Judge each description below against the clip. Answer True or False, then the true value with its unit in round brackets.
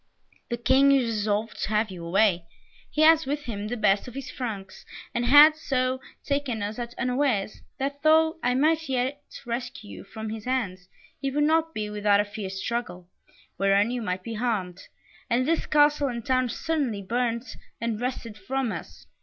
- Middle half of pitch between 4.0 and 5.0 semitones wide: True (4.7 semitones)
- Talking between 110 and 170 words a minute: False (180 wpm)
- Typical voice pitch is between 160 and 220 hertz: False (240 Hz)